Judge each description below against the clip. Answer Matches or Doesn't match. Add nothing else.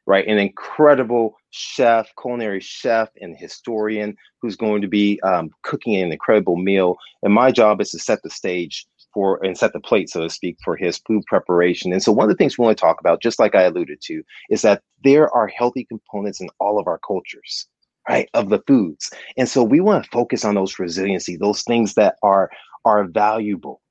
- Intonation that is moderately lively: Matches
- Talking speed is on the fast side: Matches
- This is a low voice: Matches